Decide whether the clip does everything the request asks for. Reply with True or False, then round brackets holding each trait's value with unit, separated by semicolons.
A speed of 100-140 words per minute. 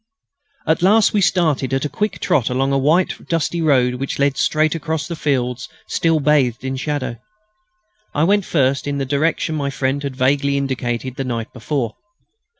False (175 wpm)